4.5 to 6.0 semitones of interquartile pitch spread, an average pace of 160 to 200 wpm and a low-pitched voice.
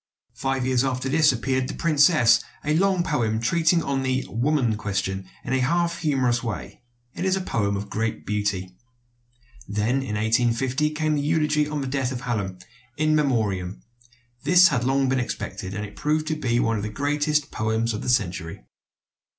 Yes: wide, 5.4 semitones; average, 180 wpm; low, 130 Hz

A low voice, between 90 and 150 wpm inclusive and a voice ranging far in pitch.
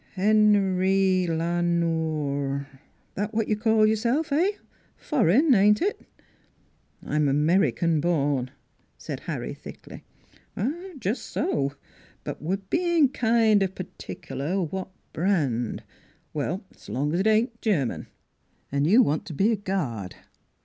No: high, 190 Hz; average, 140 wpm; wide, 6.0 semitones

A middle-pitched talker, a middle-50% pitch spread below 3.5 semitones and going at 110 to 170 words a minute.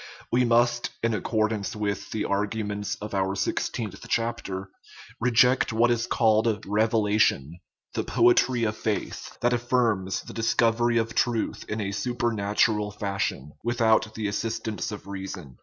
No: low, 110 Hz; narrow, 2.5 semitones; average, 145 wpm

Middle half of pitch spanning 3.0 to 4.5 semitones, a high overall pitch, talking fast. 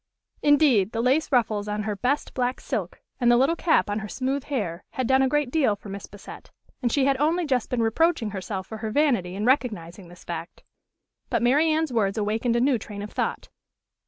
No: average, 4.9 semitones; high, 240 Hz; fast, 215 wpm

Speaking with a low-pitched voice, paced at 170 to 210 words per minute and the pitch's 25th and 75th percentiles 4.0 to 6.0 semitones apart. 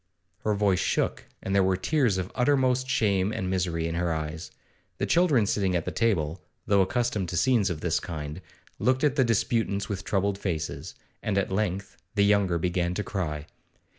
No: very low, 95 Hz; average, 185 wpm; average, 3.6 semitones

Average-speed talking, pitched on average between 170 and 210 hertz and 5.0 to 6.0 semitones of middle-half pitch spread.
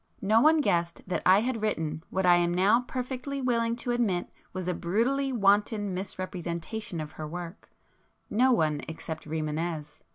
Yes: average, 155 wpm; high, 190 Hz; wide, 5.5 semitones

